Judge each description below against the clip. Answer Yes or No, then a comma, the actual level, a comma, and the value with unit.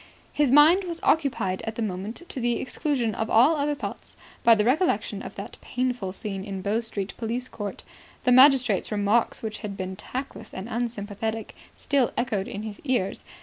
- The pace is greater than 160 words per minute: Yes, average, 180 wpm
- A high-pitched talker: Yes, high, 230 Hz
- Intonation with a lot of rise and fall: No, average, 4.1 semitones